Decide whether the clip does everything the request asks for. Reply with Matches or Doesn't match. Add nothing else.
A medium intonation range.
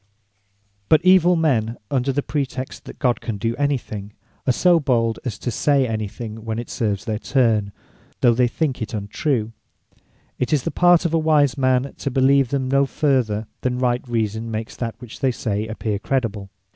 Matches